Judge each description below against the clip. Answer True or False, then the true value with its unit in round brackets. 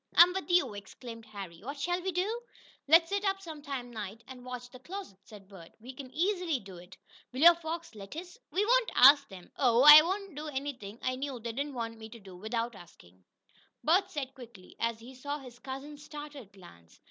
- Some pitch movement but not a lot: False (6.8 semitones)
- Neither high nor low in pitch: False (260 Hz)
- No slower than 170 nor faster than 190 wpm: False (205 wpm)